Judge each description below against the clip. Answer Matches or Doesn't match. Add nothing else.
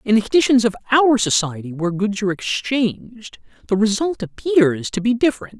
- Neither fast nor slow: Matches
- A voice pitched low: Doesn't match